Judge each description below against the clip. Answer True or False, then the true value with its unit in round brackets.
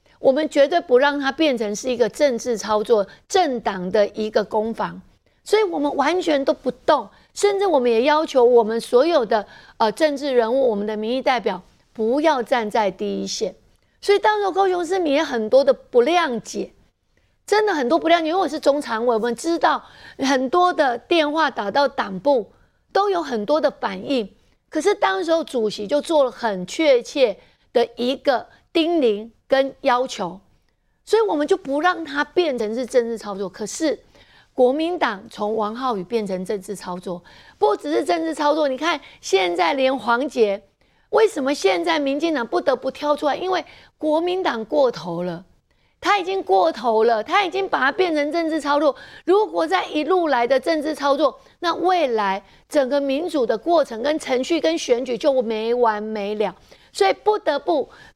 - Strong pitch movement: True (6.3 semitones)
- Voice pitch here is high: True (275 Hz)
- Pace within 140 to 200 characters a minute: False (260 characters per minute)